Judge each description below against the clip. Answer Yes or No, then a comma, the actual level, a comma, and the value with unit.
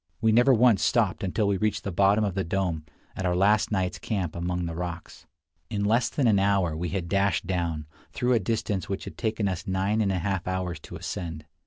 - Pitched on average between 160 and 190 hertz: No, very low, 95 Hz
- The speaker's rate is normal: No, fast, 225 wpm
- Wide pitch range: No, average, 3.1 semitones